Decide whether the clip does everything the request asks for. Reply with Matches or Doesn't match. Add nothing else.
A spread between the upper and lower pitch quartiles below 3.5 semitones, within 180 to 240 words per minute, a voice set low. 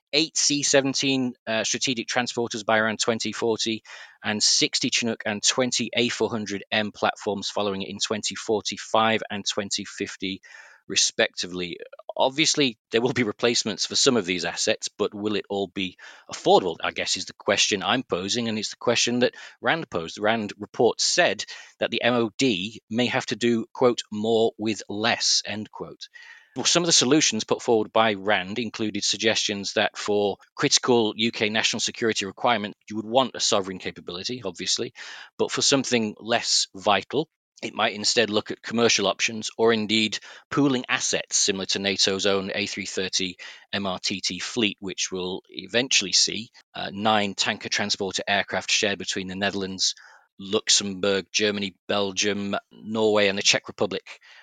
Doesn't match